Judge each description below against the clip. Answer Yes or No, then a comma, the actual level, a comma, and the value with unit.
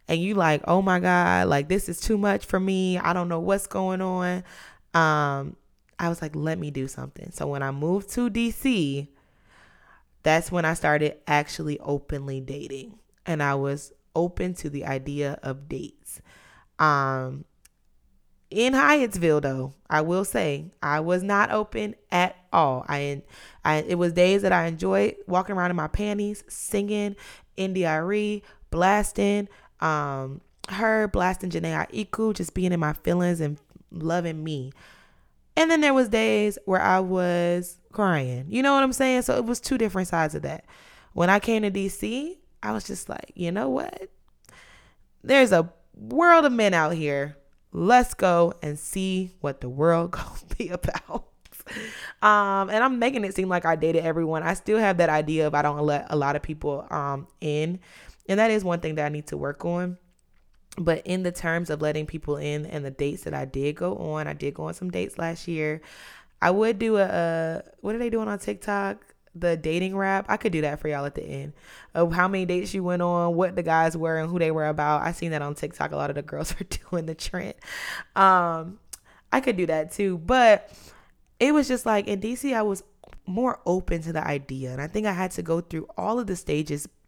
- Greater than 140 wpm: Yes, average, 200 wpm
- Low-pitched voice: No, medium, 175 Hz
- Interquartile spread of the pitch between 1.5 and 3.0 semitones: No, average, 4.8 semitones